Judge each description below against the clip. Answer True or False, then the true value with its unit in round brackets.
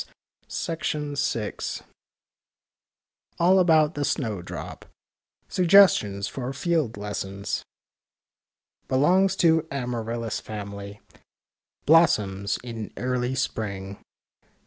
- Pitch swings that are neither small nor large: False (7.6 semitones)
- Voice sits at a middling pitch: False (125 Hz)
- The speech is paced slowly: True (75 wpm)